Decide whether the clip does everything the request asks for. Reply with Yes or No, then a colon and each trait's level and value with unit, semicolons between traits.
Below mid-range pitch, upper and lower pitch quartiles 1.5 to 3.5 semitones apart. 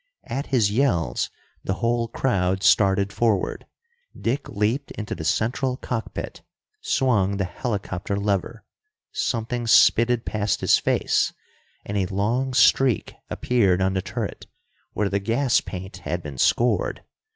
No: low, 105 Hz; average, 4.1 semitones